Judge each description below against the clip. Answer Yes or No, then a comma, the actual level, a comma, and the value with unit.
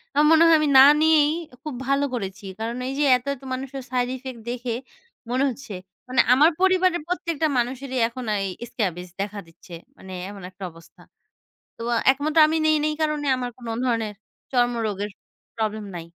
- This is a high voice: Yes, very high, 255 Hz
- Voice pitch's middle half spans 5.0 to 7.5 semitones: Yes, wide, 5.4 semitones